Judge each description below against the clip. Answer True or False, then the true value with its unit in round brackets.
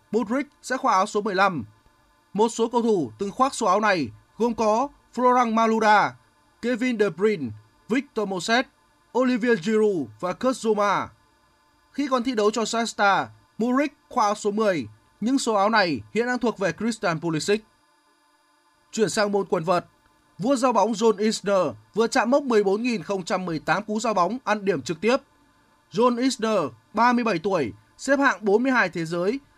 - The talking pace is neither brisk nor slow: False (160 wpm)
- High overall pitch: True (215 Hz)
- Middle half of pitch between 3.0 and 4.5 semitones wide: False (4.9 semitones)